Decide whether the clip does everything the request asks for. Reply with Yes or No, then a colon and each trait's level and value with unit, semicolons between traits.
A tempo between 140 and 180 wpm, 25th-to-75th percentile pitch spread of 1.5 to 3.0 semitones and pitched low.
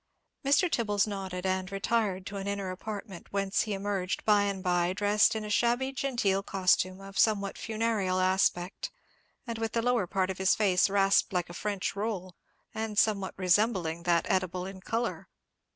No: average, 170 wpm; narrow, 2.5 semitones; high, 195 Hz